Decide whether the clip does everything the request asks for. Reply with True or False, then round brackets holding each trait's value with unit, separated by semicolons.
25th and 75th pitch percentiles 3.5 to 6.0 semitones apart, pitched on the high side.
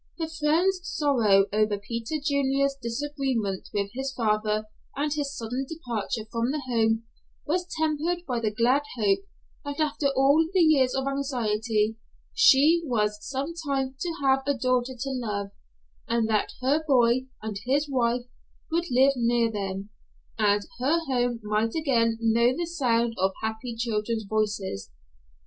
True (4.3 semitones; 245 Hz)